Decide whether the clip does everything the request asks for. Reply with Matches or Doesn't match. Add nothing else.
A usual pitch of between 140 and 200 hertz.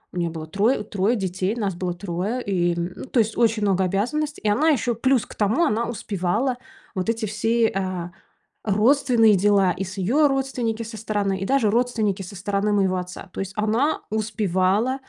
Doesn't match